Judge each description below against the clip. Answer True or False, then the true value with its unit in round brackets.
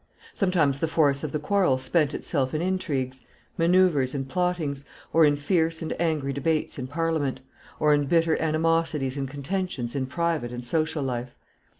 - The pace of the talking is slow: False (165 wpm)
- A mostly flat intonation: False (3.4 semitones)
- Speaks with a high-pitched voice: False (150 Hz)